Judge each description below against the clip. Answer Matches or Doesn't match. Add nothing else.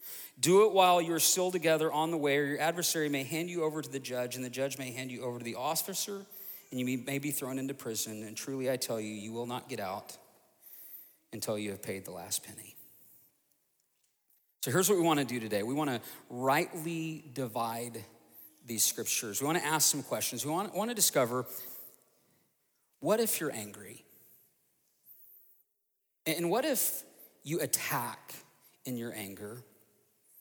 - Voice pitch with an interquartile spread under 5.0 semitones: Doesn't match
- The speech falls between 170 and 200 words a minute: Matches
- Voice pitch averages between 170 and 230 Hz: Doesn't match